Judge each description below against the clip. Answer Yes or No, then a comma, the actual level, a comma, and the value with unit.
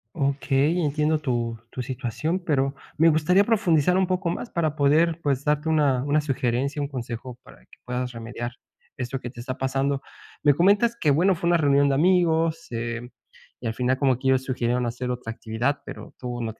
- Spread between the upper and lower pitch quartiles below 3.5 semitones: No, average, 4.3 semitones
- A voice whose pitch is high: No, medium, 140 Hz